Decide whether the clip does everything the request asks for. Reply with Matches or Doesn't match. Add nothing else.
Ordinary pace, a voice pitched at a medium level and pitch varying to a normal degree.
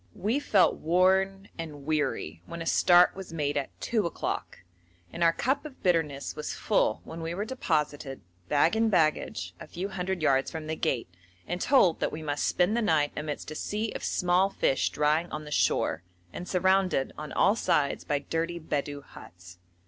Matches